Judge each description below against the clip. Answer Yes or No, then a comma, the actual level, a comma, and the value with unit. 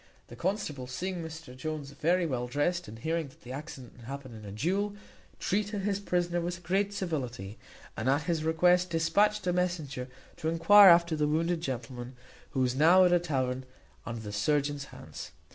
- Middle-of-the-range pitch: Yes, medium, 160 Hz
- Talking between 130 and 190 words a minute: Yes, average, 180 wpm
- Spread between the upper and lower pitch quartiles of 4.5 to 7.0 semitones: Yes, wide, 5.4 semitones